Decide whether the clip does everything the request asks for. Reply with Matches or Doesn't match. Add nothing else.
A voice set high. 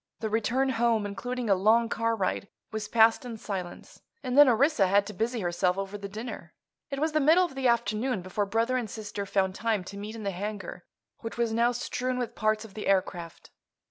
Matches